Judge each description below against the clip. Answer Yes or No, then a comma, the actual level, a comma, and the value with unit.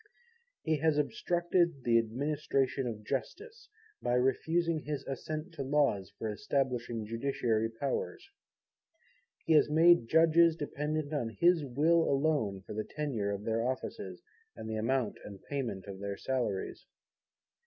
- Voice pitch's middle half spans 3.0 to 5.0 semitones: No, wide, 5.6 semitones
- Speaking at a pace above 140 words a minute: No, slow, 135 wpm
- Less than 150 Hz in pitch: Yes, low, 135 Hz